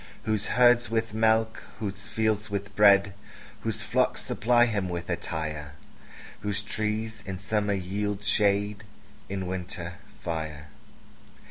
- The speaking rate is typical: No, slow, 120 wpm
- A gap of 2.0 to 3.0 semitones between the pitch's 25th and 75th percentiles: Yes, average, 2.7 semitones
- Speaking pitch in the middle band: No, low, 100 Hz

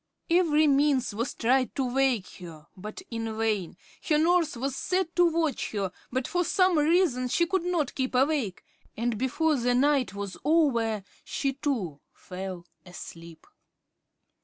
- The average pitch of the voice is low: No, very high, 260 Hz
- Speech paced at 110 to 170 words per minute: Yes, average, 150 wpm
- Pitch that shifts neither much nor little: No, wide, 6.3 semitones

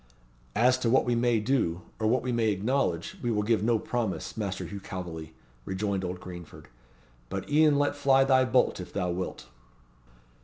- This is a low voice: Yes, low, 110 Hz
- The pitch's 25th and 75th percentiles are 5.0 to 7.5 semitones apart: Yes, wide, 5.4 semitones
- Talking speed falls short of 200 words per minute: Yes, average, 180 wpm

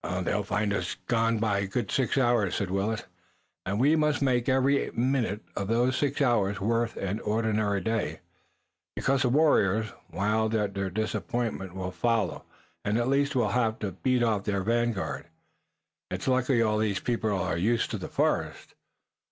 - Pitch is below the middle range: Yes, low, 110 Hz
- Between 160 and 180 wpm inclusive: Yes, average, 170 wpm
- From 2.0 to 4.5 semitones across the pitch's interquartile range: Yes, average, 3.4 semitones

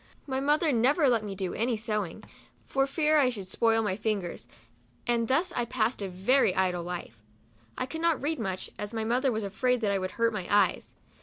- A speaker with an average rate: No, fast, 210 wpm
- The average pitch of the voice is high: Yes, high, 225 Hz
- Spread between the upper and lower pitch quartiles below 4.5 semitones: No, average, 5.0 semitones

